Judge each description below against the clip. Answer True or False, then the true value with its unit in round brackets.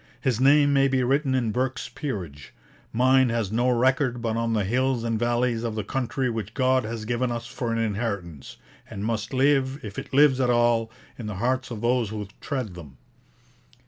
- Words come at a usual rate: True (195 wpm)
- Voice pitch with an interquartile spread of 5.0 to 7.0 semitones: False (2.9 semitones)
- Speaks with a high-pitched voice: False (120 Hz)